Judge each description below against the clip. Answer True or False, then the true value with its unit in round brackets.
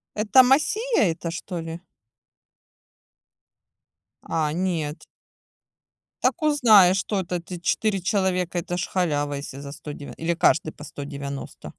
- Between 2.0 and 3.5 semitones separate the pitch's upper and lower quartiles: False (4.2 semitones)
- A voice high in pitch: False (175 Hz)